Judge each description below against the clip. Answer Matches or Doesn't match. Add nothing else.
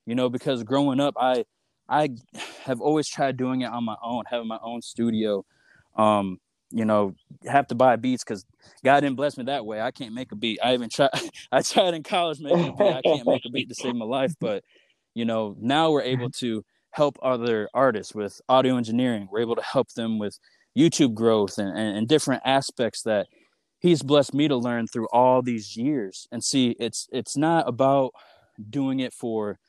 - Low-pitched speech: Matches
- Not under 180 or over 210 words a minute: Matches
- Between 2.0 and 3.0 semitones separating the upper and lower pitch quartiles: Doesn't match